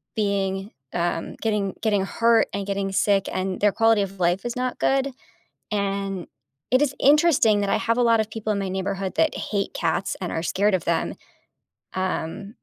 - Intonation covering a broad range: No, average, 2.7 semitones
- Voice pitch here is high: Yes, high, 200 Hz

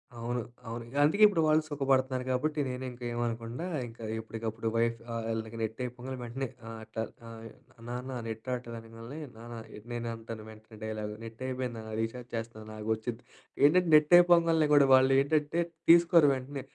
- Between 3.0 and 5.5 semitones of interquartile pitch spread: Yes, average, 3.5 semitones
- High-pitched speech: No, low, 120 Hz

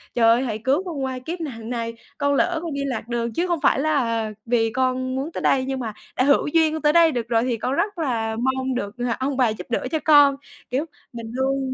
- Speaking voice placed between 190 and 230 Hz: No, very high, 260 Hz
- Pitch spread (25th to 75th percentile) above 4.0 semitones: No, average, 3.7 semitones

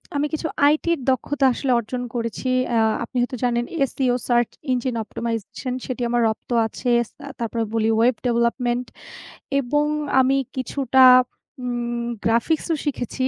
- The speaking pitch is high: Yes, high, 245 Hz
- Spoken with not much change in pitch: Yes, narrow, 2.0 semitones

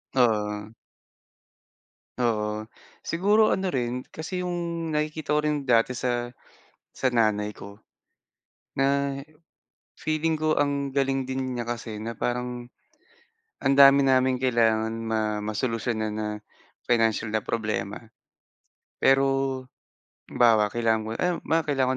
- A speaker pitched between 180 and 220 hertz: No, low, 125 Hz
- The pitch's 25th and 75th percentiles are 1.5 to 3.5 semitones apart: No, average, 4.0 semitones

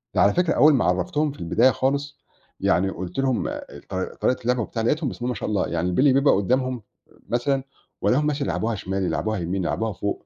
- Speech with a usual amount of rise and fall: No, wide, 5.9 semitones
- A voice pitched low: Yes, low, 120 Hz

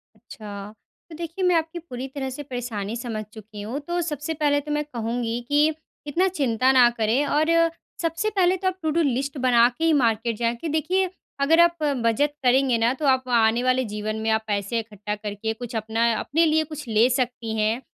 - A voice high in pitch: Yes, very high, 255 Hz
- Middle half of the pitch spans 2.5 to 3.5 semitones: No, wide, 5.5 semitones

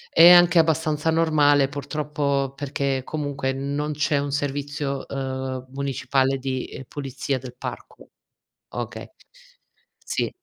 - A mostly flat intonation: Yes, narrow, 1.8 semitones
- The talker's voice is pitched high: No, medium, 140 Hz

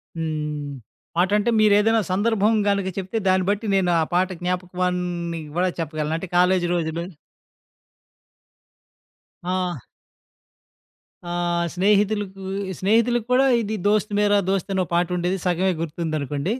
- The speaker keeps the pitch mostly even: No, average, 3.2 semitones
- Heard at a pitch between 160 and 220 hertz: Yes, medium, 185 Hz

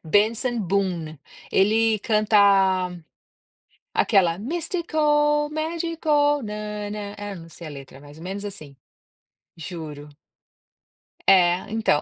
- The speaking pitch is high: Yes, high, 205 Hz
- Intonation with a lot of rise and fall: Yes, wide, 8.9 semitones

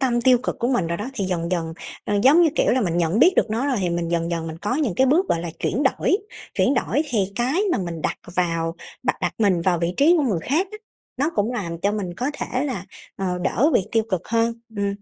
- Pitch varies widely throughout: Yes, wide, 7.1 semitones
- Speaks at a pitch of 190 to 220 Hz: Yes, high, 210 Hz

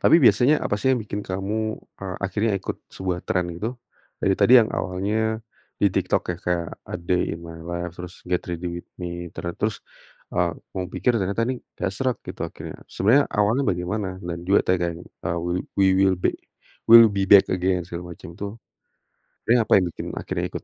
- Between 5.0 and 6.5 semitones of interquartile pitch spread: No, average, 3.2 semitones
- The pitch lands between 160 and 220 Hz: No, very low, 95 Hz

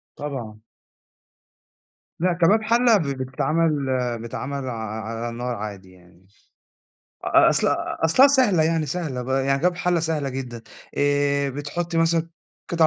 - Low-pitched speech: No, medium, 145 Hz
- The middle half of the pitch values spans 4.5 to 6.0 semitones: Yes, wide, 5.4 semitones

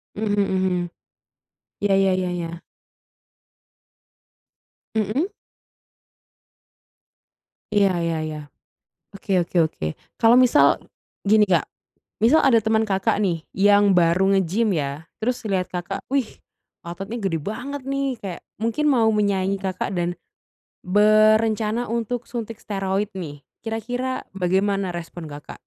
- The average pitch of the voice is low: No, high, 205 Hz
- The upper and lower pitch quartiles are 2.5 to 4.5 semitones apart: Yes, average, 3.5 semitones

